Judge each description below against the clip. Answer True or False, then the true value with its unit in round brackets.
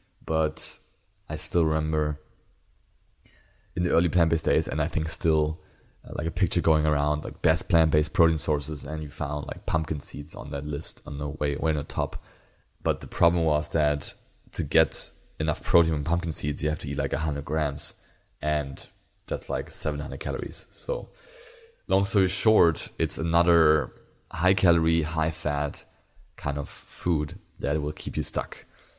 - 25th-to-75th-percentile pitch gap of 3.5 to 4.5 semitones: False (2.6 semitones)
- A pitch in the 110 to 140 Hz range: False (80 Hz)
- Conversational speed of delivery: True (175 wpm)